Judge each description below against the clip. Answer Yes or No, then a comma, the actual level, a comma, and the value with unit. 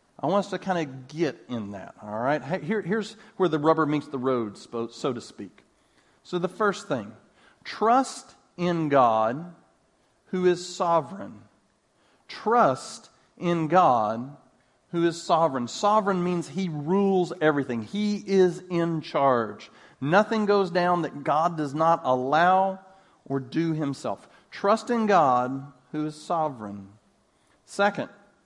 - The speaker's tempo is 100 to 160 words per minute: Yes, slow, 135 wpm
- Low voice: No, medium, 170 Hz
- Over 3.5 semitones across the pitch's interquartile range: Yes, average, 5.3 semitones